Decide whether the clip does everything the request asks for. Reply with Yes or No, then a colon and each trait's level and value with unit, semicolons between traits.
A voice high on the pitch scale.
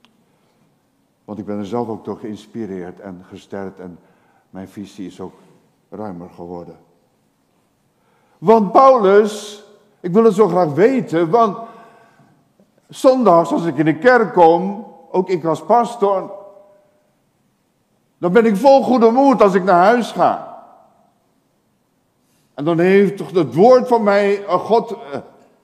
Yes: high, 195 Hz